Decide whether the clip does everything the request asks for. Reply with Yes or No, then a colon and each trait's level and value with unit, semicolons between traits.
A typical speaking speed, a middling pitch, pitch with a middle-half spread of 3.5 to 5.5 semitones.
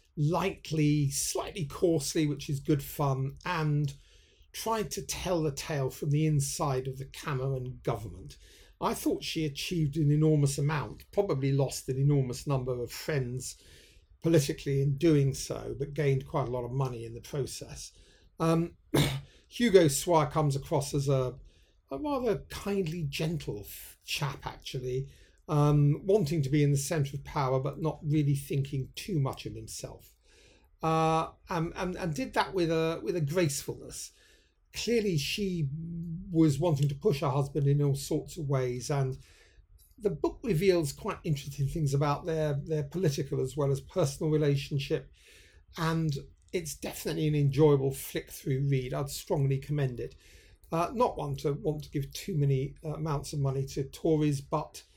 No: average, 160 wpm; medium, 145 Hz; average, 2.9 semitones